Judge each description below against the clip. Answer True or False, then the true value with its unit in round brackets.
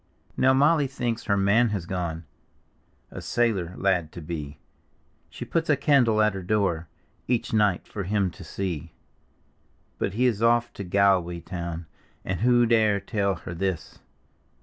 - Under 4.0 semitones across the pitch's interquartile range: False (4.9 semitones)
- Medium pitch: False (100 Hz)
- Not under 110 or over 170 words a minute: True (155 wpm)